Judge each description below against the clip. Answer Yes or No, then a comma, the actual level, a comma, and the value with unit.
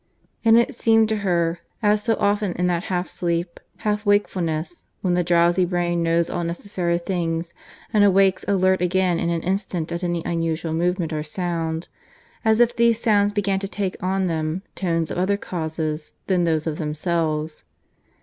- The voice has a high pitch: No, medium, 175 Hz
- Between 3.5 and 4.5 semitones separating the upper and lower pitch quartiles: No, average, 3.0 semitones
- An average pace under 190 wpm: Yes, average, 170 wpm